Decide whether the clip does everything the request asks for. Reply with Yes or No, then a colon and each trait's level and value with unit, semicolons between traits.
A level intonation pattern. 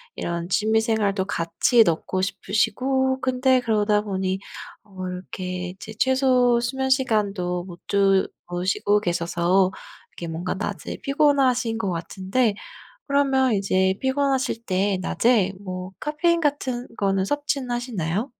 No: wide, 5.6 semitones